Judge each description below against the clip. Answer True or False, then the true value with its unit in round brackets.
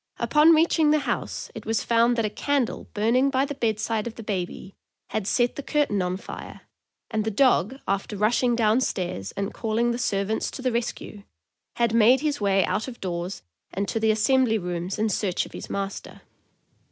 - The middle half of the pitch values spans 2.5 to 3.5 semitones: False (4.0 semitones)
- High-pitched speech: True (220 Hz)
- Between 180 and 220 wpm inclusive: True (195 wpm)